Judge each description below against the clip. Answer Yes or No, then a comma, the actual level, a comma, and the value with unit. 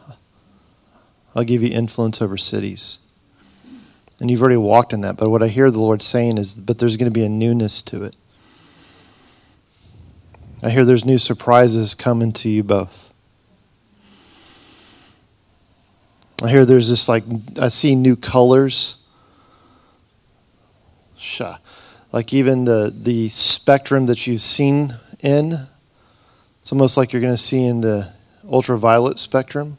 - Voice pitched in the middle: No, low, 115 Hz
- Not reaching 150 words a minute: Yes, slow, 135 wpm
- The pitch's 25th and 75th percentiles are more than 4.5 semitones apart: No, average, 3.3 semitones